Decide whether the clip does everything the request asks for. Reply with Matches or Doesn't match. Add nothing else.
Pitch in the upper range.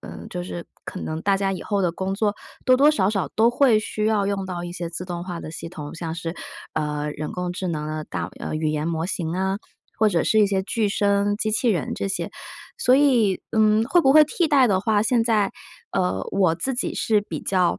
Matches